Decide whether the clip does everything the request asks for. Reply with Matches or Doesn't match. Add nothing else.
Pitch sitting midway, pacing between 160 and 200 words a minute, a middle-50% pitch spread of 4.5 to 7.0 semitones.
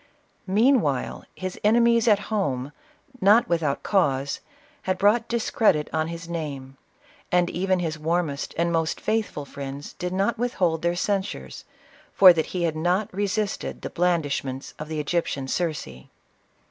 Doesn't match